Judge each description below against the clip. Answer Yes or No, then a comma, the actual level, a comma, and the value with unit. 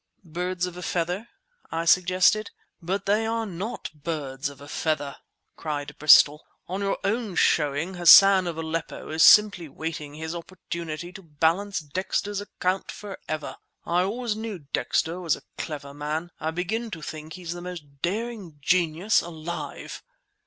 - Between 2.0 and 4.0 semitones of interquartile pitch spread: Yes, average, 3.7 semitones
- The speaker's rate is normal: Yes, average, 150 wpm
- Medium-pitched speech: Yes, medium, 175 Hz